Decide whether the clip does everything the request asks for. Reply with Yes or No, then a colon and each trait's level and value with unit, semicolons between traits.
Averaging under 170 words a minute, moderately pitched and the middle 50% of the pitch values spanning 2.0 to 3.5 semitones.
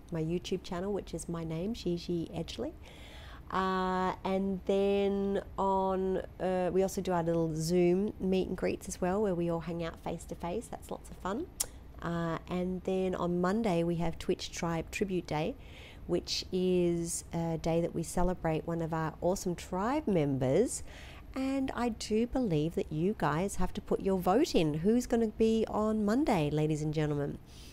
No: average, 180 wpm; medium, 180 Hz; average, 2.8 semitones